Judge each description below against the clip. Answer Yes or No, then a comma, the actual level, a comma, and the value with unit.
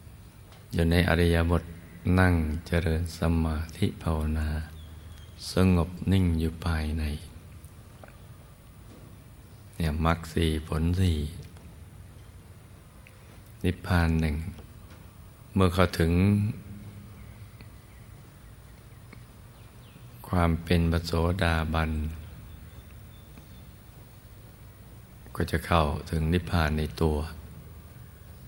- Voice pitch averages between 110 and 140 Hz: No, very low, 90 Hz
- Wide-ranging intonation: No, average, 4.3 semitones